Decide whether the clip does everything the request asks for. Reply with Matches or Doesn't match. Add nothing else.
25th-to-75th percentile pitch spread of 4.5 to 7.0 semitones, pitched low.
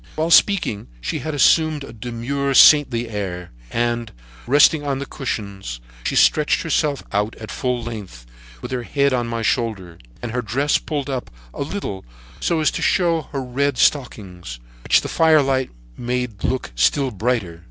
Matches